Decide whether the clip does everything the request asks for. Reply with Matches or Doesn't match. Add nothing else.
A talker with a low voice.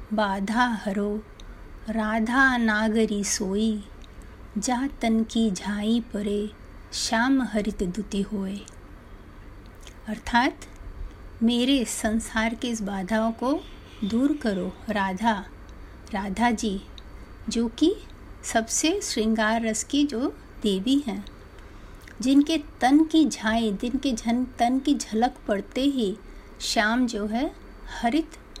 Doesn't match